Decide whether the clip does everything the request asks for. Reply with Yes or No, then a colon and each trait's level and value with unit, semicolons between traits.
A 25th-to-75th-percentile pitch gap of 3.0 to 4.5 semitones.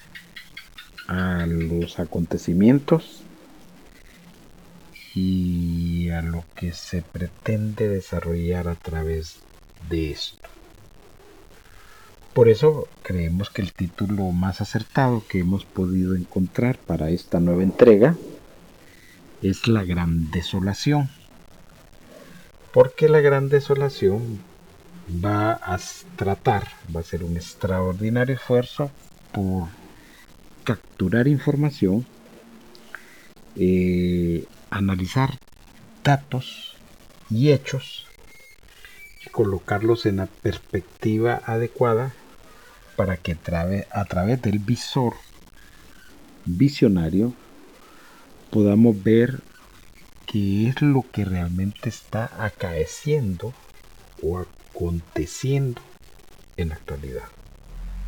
No: average, 5.3 semitones